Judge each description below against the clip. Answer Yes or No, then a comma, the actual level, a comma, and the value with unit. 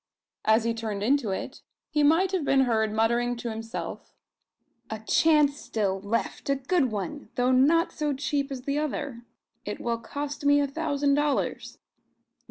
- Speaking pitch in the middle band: No, very high, 270 Hz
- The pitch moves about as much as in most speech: Yes, average, 4.2 semitones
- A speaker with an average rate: Yes, average, 165 wpm